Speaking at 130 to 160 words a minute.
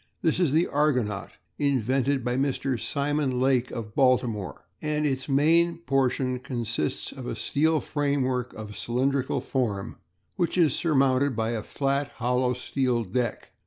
Yes: average, 140 wpm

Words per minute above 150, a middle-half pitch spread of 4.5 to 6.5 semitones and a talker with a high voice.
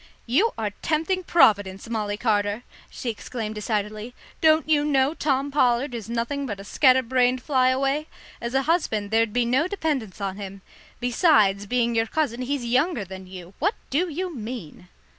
Yes: average, 170 wpm; average, 5.2 semitones; high, 245 Hz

